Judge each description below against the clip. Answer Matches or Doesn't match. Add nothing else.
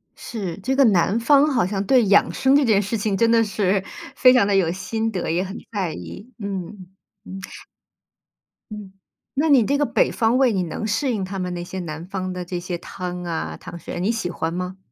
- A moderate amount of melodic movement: Matches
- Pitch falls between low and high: Doesn't match